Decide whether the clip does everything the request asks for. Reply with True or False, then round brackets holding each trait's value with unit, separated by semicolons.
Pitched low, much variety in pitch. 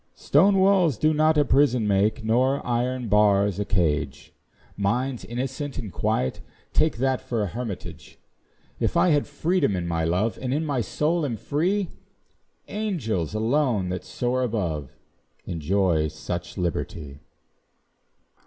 True (115 Hz; 7.4 semitones)